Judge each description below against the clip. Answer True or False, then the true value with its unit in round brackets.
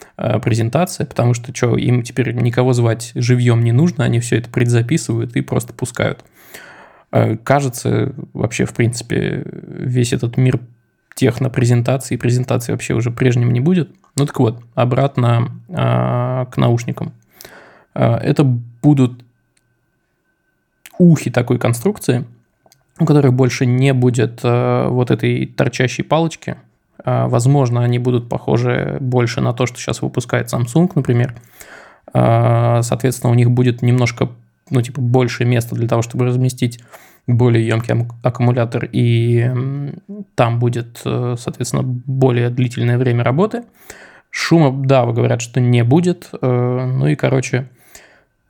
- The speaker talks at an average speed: True (120 wpm)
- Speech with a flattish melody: True (1.9 semitones)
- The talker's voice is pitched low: True (125 Hz)